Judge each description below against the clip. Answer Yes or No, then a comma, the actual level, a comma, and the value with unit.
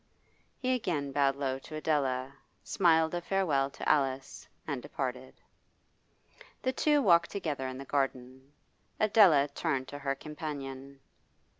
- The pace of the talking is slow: Yes, slow, 130 wpm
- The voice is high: No, medium, 140 Hz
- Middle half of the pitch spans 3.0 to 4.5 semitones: Yes, average, 3.5 semitones